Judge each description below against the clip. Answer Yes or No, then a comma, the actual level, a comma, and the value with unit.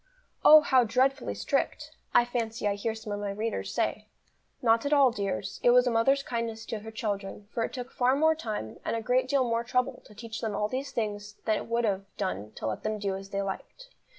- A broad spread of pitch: No, average, 3.4 semitones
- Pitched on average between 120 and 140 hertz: No, high, 225 Hz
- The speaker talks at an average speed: No, fast, 235 wpm